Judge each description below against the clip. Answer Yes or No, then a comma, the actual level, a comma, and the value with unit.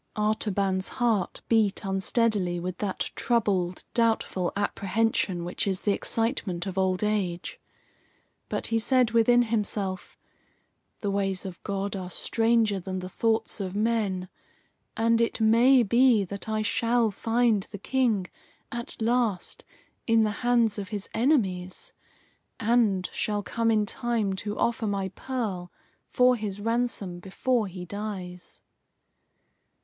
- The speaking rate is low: Yes, slow, 130 wpm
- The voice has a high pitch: Yes, high, 210 Hz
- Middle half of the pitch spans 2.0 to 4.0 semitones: Yes, average, 3.3 semitones